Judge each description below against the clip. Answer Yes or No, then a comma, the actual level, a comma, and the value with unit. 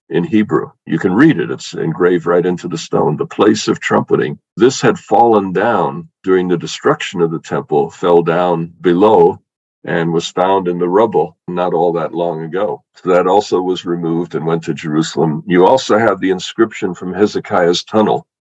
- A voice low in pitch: Yes, very low, 85 Hz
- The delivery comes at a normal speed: Yes, average, 185 wpm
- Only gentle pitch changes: Yes, narrow, 1.6 semitones